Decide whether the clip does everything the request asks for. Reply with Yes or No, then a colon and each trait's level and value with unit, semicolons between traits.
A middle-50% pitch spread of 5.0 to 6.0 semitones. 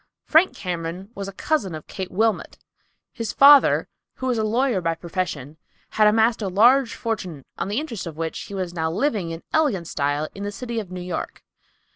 Yes: average, 5.3 semitones